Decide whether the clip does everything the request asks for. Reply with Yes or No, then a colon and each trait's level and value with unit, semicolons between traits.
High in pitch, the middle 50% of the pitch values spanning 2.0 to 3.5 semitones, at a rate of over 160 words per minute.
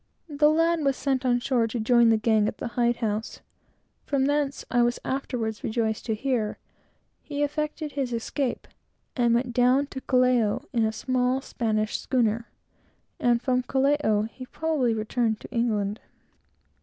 No: high, 245 Hz; average, 3.2 semitones; average, 155 wpm